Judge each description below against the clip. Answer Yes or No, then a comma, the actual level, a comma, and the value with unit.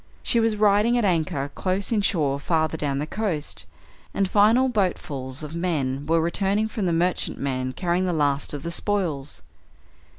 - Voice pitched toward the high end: No, medium, 170 Hz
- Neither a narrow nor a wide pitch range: No, wide, 5.7 semitones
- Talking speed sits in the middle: Yes, average, 160 wpm